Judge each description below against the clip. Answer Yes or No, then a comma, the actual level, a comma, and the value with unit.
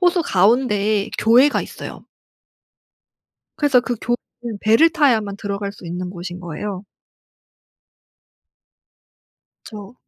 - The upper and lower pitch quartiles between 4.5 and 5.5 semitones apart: No, average, 3.9 semitones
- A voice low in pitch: No, high, 210 Hz